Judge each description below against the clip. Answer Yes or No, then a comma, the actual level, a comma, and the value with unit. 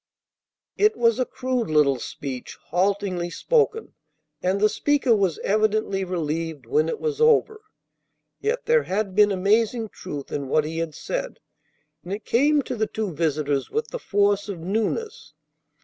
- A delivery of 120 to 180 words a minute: Yes, average, 155 wpm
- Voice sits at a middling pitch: No, high, 205 Hz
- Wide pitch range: Yes, wide, 7.7 semitones